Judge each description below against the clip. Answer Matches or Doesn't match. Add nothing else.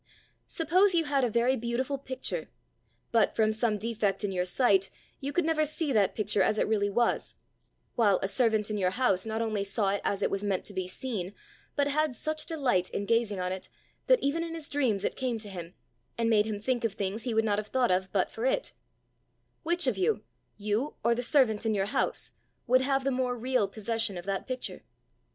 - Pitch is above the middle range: Matches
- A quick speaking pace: Matches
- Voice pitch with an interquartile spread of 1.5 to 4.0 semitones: Doesn't match